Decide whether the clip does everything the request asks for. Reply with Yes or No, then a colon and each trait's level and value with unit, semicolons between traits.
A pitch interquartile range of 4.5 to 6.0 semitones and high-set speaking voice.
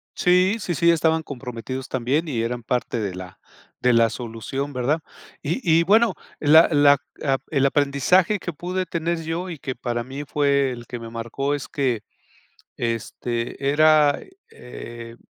No: average, 5.1 semitones; medium, 140 Hz